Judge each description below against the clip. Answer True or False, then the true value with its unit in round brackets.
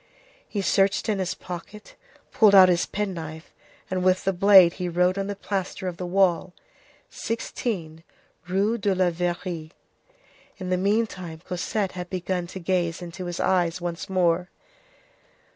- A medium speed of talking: True (150 wpm)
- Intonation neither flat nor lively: False (1.9 semitones)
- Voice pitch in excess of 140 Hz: True (185 Hz)